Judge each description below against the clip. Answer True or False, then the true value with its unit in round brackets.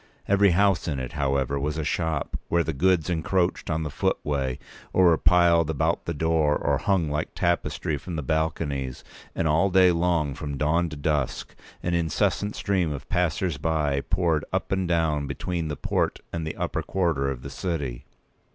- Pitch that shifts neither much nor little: True (3.1 semitones)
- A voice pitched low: True (80 Hz)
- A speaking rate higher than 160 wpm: True (185 wpm)